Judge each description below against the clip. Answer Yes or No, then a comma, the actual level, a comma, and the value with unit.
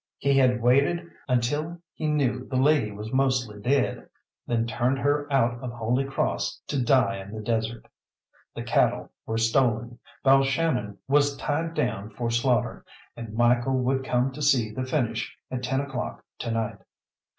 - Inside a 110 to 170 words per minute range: Yes, average, 160 wpm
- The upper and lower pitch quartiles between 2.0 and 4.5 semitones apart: Yes, average, 2.8 semitones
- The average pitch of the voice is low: Yes, low, 125 Hz